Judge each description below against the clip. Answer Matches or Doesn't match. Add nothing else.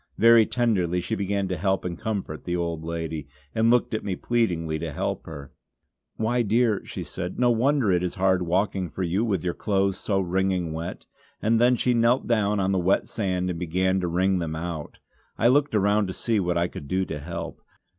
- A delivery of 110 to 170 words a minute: Doesn't match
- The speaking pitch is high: Doesn't match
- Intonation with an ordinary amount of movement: Matches